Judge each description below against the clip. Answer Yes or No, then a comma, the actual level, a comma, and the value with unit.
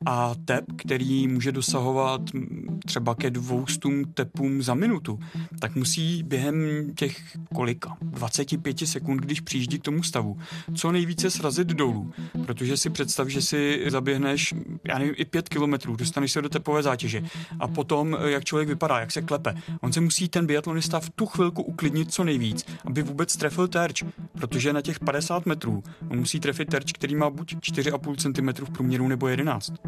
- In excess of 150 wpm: Yes, fast, 170 wpm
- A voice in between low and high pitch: Yes, medium, 145 Hz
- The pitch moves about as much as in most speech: Yes, average, 3.6 semitones